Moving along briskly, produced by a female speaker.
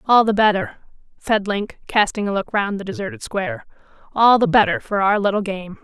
No: average, 195 wpm; female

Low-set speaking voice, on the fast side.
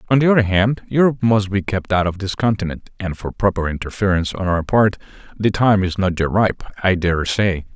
Yes: low, 100 Hz; fast, 215 wpm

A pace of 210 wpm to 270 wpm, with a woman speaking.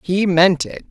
No: average, 200 wpm; female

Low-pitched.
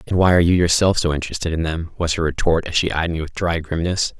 Yes: very low, 85 Hz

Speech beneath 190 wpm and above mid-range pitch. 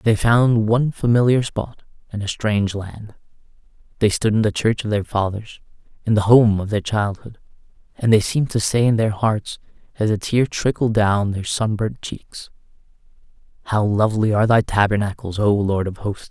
No: average, 180 wpm; low, 110 Hz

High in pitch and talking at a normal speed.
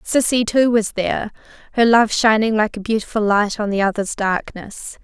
Yes: high, 215 Hz; average, 180 wpm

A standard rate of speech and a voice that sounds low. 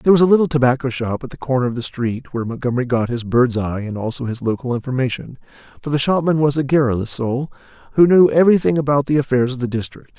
No: fast, 230 wpm; low, 130 Hz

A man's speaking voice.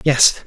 Yes: male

